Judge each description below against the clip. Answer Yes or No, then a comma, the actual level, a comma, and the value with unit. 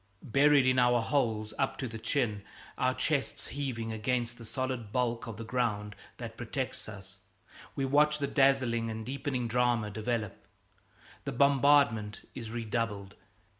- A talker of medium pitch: No, low, 120 Hz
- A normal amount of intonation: Yes, average, 3.2 semitones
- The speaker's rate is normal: Yes, average, 145 wpm